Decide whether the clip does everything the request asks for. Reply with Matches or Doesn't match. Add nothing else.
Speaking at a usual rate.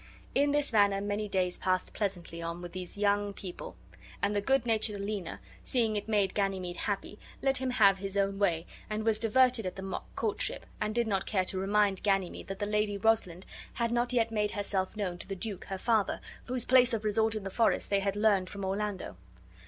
Doesn't match